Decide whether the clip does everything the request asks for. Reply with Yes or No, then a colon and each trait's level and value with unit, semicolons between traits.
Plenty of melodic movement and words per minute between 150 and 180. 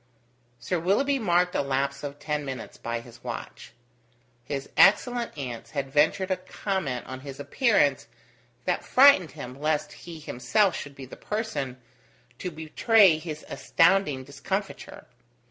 No: wide, 5.8 semitones; average, 140 wpm